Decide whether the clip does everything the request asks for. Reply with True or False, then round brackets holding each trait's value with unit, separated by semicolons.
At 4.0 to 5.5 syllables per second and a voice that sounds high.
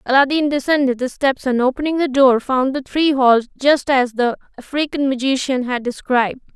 True (5.3 syllables/s; 265 Hz)